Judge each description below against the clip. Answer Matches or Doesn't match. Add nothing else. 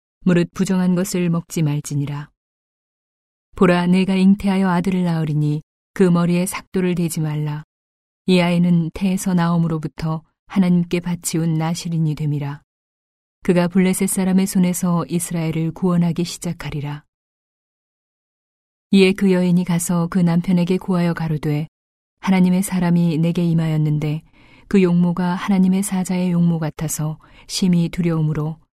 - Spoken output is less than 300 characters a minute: Doesn't match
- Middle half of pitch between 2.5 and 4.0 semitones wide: Matches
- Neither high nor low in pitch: Matches